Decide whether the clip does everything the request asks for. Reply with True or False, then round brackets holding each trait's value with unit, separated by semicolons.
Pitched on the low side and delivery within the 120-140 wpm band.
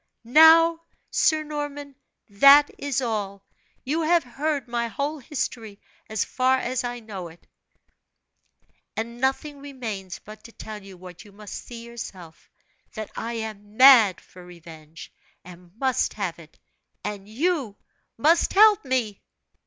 False (235 Hz; 135 wpm)